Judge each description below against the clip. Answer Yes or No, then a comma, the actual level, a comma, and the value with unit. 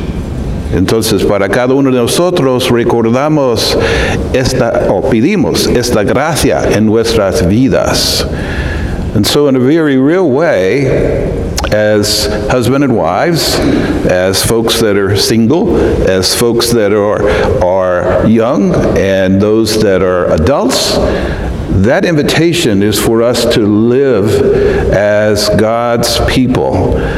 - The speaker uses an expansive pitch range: No, average, 4.0 semitones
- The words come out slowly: Yes, slow, 115 wpm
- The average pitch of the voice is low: Yes, low, 105 Hz